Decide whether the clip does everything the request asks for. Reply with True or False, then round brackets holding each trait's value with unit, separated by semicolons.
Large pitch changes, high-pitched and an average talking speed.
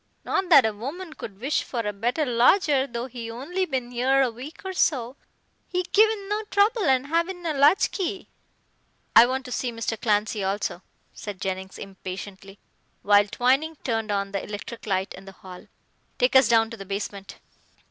True (6.8 semitones; 245 Hz; 180 wpm)